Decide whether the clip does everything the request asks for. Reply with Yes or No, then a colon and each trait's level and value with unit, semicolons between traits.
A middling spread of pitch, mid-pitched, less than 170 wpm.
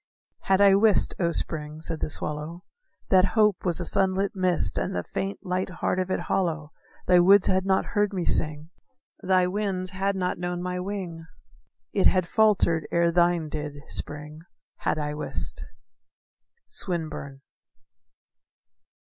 Yes: average, 3.2 semitones; medium, 180 Hz; average, 150 wpm